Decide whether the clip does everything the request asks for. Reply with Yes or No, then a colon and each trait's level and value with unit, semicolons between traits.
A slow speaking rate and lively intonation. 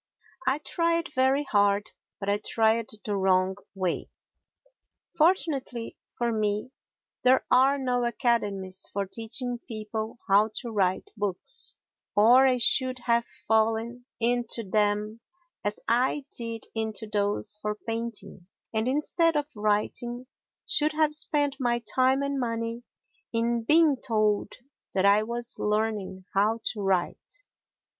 No: slow, 125 wpm; average, 3.5 semitones